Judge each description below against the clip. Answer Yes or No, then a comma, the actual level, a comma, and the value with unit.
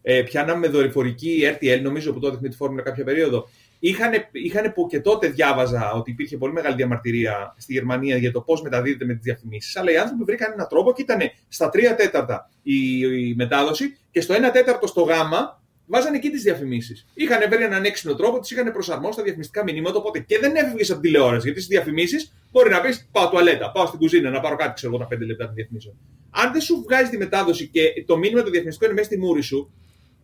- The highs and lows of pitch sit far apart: Yes, wide, 9.0 semitones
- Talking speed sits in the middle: No, fast, 220 wpm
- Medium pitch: Yes, medium, 155 Hz